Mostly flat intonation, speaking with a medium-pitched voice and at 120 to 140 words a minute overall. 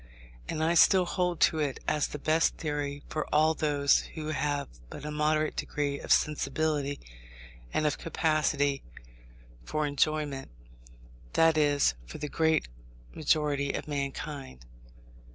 Yes: narrow, 1.6 semitones; medium, 150 Hz; slow, 135 wpm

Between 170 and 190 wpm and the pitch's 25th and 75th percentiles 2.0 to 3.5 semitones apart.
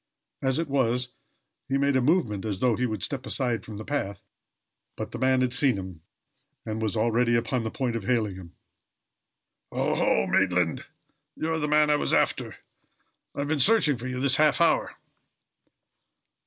No: average, 175 wpm; average, 4.4 semitones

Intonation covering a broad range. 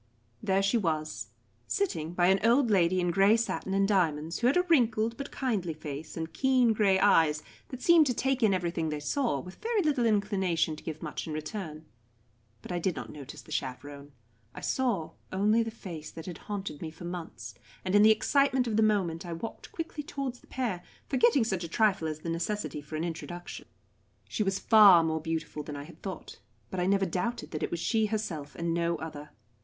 Yes: wide, 5.7 semitones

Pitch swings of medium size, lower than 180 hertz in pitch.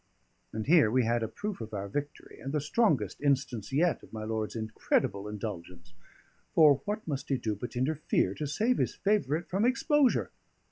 No: wide, 7.0 semitones; low, 135 Hz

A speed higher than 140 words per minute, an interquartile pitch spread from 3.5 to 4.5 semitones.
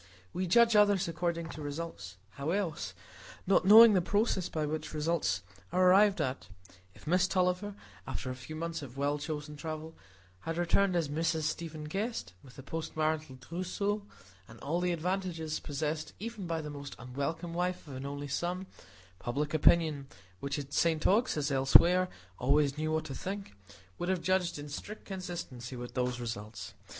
Yes: average, 170 wpm; average, 4.2 semitones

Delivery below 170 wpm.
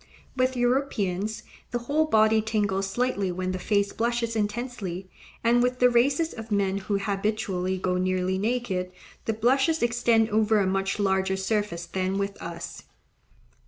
Yes: average, 150 wpm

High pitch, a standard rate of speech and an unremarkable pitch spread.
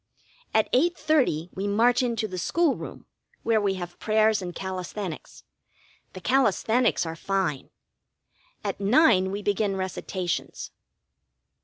No: high, 200 Hz; slow, 120 wpm; average, 3.8 semitones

